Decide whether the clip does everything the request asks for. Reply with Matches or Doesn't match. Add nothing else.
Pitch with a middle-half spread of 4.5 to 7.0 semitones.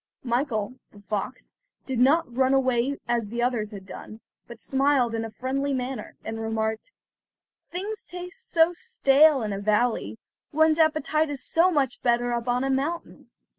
Matches